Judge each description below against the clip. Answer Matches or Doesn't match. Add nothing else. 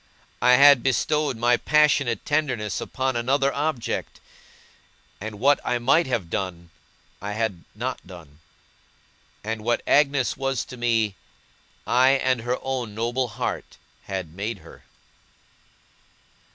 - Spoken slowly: Matches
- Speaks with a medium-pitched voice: Doesn't match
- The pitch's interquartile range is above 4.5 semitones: Doesn't match